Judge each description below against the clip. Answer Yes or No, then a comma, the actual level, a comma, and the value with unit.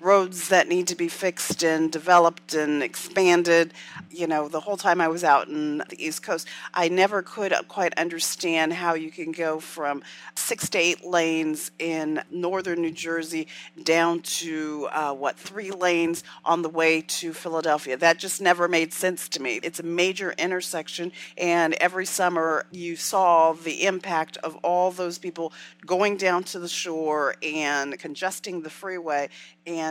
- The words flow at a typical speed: Yes, average, 165 wpm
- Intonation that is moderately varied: No, narrow, 2.0 semitones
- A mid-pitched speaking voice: Yes, medium, 170 Hz